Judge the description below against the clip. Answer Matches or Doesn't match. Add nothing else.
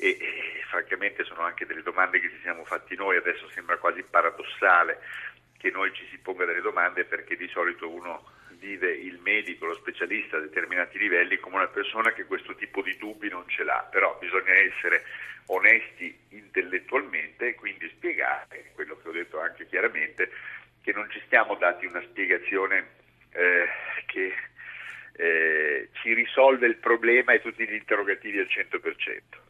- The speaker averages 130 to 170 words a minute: Matches